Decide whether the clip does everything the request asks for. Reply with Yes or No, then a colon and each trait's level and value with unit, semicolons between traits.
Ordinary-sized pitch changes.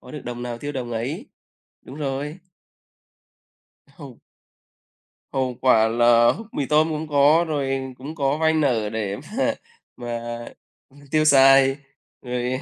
Yes: average, 3.7 semitones